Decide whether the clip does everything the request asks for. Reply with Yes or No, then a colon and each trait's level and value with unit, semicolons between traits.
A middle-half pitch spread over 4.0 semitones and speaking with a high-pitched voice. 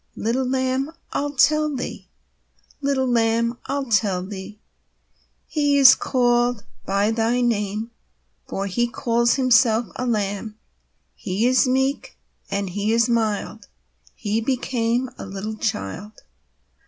No: average, 3.6 semitones; high, 235 Hz